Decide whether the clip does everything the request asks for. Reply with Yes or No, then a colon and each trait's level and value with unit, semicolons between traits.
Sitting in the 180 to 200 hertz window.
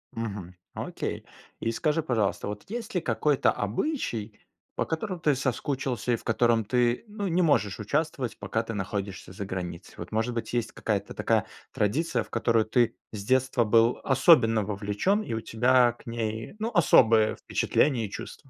No: low, 115 Hz